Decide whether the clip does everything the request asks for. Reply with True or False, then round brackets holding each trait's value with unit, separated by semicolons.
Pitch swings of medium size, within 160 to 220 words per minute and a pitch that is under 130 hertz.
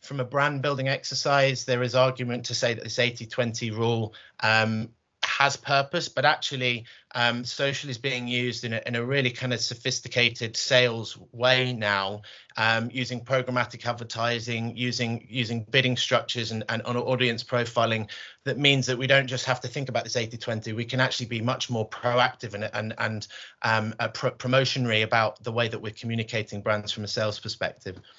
False (2.2 semitones; 180 wpm; 120 Hz)